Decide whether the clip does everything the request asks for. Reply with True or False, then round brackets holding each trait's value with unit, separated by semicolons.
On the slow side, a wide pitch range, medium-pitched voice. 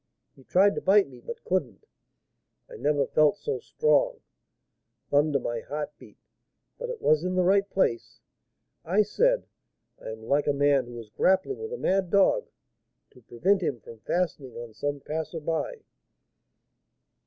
False (160 wpm; 6.6 semitones; 160 Hz)